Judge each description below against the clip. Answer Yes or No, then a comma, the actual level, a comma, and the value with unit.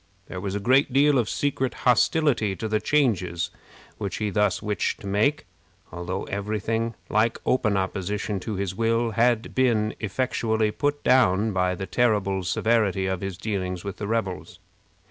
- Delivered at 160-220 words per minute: Yes, average, 165 wpm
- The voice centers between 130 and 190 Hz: No, low, 105 Hz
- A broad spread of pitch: No, average, 3.3 semitones